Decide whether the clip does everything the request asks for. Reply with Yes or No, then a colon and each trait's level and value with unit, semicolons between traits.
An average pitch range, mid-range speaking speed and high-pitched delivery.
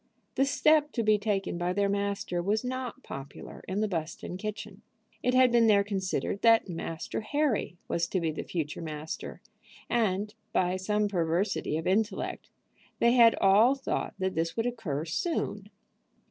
Yes: average, 4.4 semitones; average, 160 wpm; high, 200 Hz